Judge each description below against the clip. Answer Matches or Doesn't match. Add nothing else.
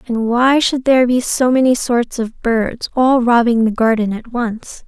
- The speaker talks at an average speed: Matches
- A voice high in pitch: Matches